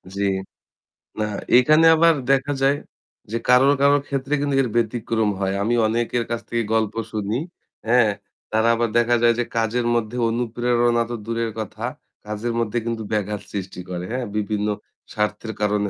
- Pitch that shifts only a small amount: Yes, narrow, 2.3 semitones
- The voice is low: Yes, low, 115 Hz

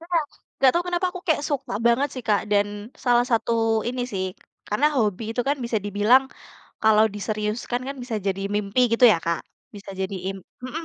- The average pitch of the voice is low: No, high, 230 Hz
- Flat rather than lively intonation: No, average, 3.9 semitones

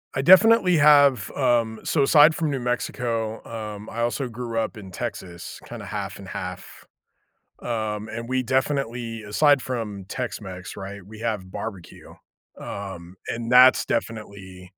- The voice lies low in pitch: Yes, low, 115 Hz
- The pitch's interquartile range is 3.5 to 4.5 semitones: Yes, average, 4.0 semitones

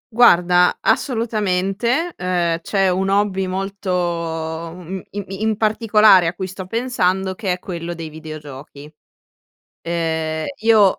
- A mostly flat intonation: No, average, 3.4 semitones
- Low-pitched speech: No, medium, 185 Hz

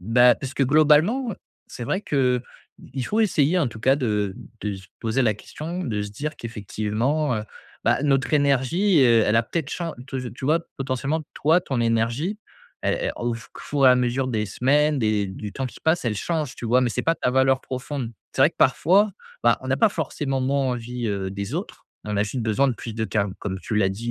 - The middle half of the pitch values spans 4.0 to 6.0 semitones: Yes, average, 4.8 semitones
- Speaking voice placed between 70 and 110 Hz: No, low, 130 Hz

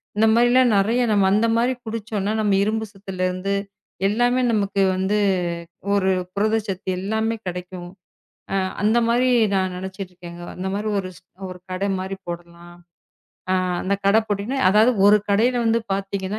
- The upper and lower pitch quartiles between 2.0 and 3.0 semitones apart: Yes, average, 2.7 semitones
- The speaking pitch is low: No, high, 200 Hz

